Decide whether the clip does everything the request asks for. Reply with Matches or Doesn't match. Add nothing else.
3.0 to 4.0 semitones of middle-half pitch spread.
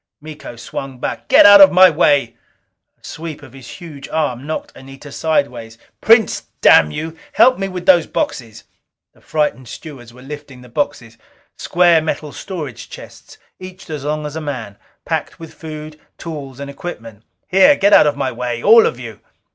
Doesn't match